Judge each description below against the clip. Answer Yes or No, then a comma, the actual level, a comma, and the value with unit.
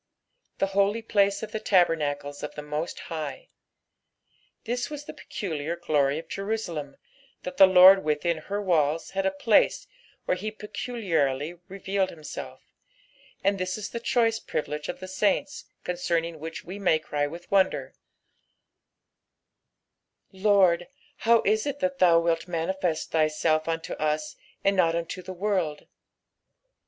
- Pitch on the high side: No, medium, 180 Hz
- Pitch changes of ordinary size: Yes, average, 4.1 semitones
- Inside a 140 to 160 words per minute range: Yes, average, 145 wpm